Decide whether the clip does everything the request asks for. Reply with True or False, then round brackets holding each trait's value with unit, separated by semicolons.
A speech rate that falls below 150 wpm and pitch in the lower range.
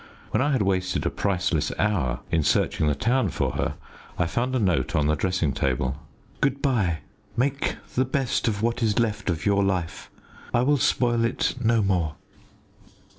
False (180 wpm; 100 Hz)